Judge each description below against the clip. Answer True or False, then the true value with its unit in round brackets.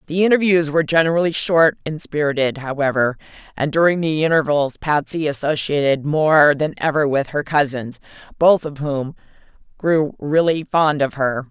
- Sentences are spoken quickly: False (145 wpm)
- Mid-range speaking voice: True (150 Hz)